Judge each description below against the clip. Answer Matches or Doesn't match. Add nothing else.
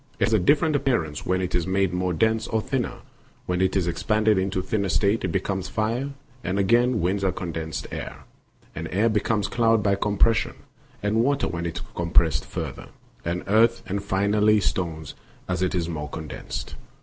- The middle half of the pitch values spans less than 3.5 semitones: Doesn't match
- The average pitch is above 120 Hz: Doesn't match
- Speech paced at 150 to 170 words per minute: Doesn't match